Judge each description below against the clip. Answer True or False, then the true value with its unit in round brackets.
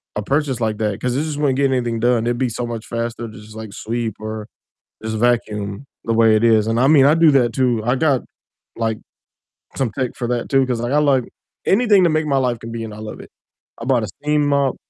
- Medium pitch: False (120 Hz)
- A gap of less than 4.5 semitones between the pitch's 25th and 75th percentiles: True (3.4 semitones)